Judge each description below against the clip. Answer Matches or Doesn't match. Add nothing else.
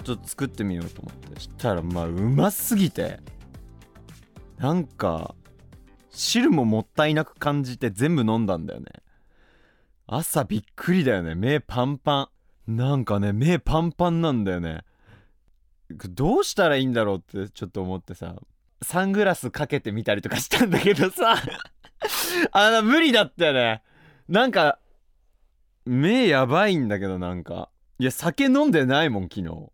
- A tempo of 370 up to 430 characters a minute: Doesn't match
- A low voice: Matches